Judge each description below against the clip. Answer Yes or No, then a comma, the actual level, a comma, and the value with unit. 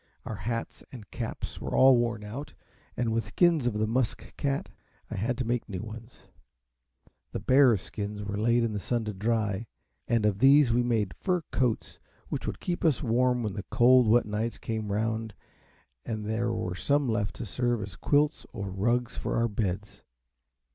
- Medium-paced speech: Yes, average, 185 wpm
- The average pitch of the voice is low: Yes, low, 115 Hz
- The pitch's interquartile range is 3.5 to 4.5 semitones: No, average, 2.8 semitones